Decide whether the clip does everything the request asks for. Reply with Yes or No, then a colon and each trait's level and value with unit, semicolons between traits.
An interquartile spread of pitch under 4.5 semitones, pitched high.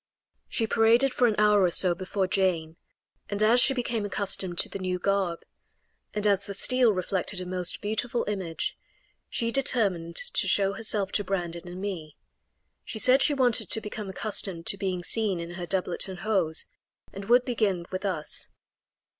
Yes: average, 3.3 semitones; high, 195 Hz